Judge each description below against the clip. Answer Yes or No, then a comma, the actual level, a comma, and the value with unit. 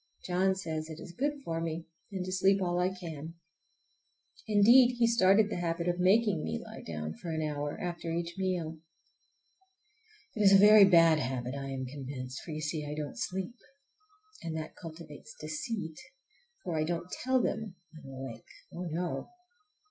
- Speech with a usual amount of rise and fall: Yes, average, 3.8 semitones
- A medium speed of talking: Yes, average, 170 wpm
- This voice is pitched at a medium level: Yes, medium, 170 Hz